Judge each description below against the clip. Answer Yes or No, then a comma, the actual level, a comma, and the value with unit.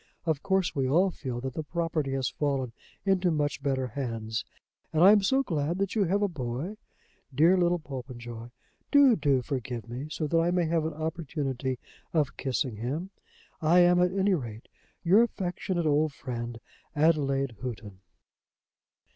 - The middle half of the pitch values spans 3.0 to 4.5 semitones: No, average, 5.3 semitones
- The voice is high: No, medium, 150 Hz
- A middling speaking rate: Yes, average, 165 wpm